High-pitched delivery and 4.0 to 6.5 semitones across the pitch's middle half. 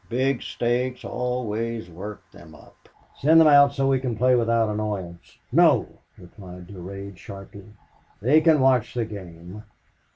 No: low, 115 Hz; average, 4.5 semitones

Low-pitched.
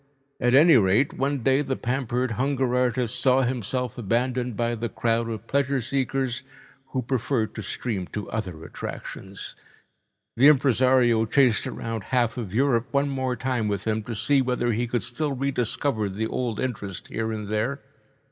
Yes: low, 120 Hz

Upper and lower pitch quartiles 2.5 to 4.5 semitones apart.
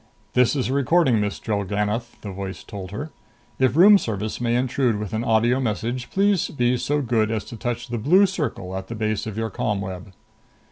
Yes: average, 3.8 semitones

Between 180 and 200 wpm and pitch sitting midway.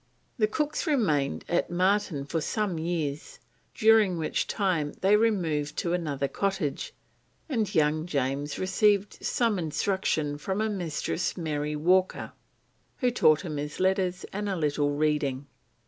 No: slow, 135 wpm; medium, 175 Hz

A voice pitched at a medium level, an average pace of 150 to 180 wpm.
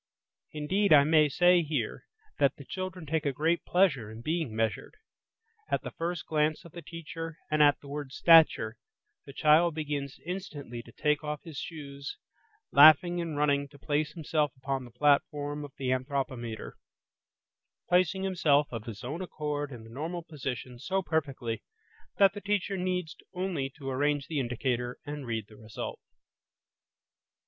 Yes: medium, 150 Hz; average, 160 wpm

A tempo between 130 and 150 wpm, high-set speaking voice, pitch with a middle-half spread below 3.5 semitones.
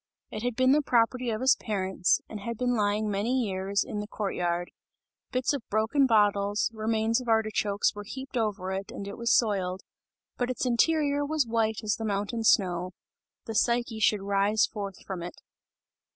No: average, 180 wpm; high, 215 Hz; average, 3.0 semitones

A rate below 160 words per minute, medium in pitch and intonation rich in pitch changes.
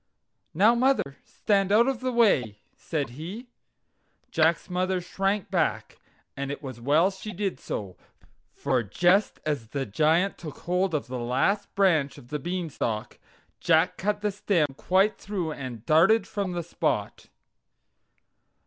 Yes: average, 145 wpm; medium, 175 Hz; wide, 6.1 semitones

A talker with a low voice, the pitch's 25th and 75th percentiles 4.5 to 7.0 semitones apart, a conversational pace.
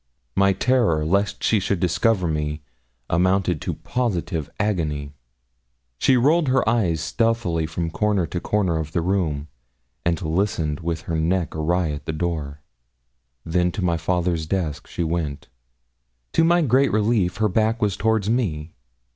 Yes: very low, 90 Hz; average, 4.9 semitones; average, 150 wpm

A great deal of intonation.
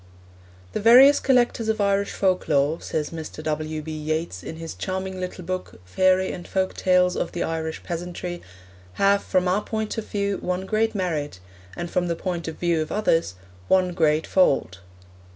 No: average, 3.2 semitones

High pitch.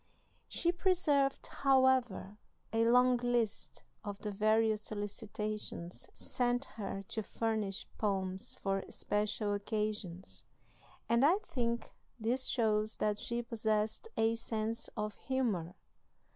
Yes: high, 220 Hz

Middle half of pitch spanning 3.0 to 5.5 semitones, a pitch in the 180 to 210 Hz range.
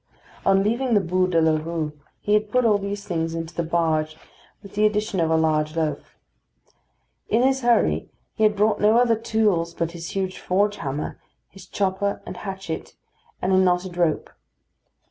Yes: average, 4.1 semitones; high, 190 Hz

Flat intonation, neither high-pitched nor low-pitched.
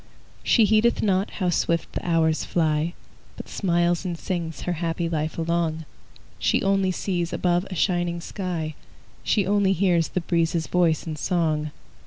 Yes: narrow, 2.2 semitones; medium, 170 Hz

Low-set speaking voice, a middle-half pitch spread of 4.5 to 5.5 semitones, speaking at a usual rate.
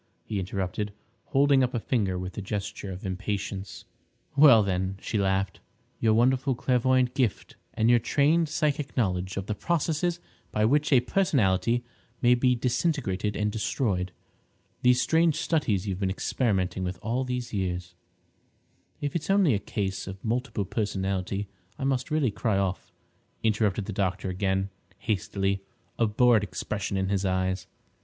Yes: low, 105 Hz; average, 4.9 semitones; average, 150 wpm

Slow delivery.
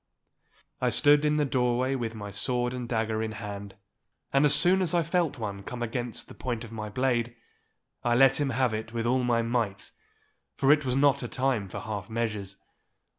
No: average, 200 wpm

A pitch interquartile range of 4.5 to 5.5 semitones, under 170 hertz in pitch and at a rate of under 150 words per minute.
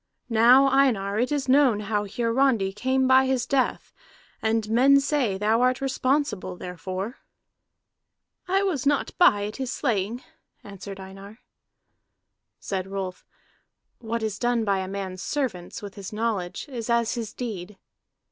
No: average, 4.9 semitones; high, 225 Hz; average, 140 wpm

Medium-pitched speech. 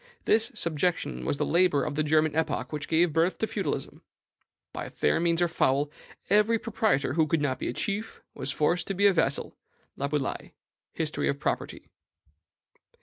Yes: medium, 160 Hz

